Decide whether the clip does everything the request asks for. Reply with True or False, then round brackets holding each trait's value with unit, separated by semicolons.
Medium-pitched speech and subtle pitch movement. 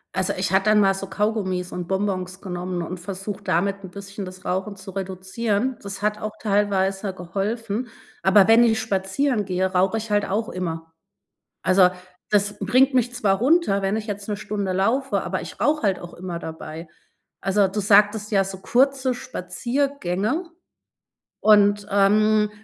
False (200 Hz; 2.3 semitones)